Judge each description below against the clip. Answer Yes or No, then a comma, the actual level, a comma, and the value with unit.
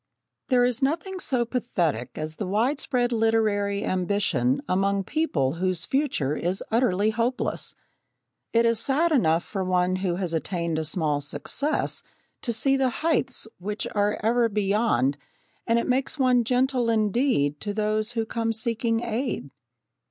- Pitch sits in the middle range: No, high, 220 Hz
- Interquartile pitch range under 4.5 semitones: No, average, 5.1 semitones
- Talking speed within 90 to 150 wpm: Yes, average, 145 wpm